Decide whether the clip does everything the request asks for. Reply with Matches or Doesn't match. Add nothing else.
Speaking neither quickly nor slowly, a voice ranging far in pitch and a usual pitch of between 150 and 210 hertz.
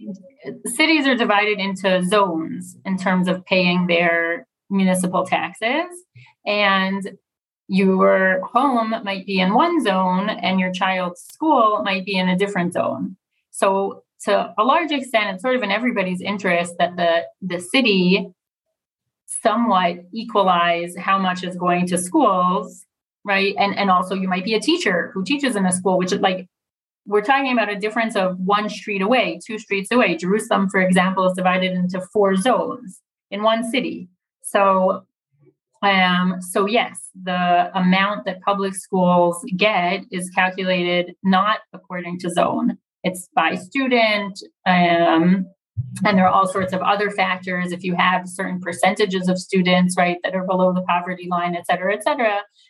Doesn't match